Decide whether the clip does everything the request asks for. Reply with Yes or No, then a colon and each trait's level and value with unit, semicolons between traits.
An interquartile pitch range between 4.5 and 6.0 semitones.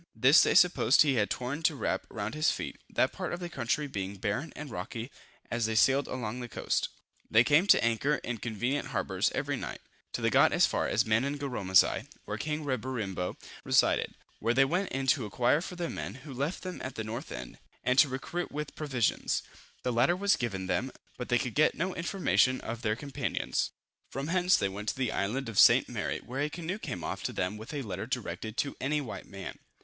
Yes: average, 5.1 semitones